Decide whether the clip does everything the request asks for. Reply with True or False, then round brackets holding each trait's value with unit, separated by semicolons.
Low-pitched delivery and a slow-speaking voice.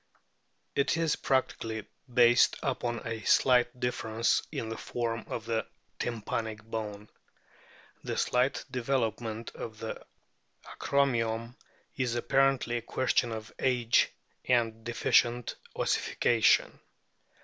True (120 Hz; 105 wpm)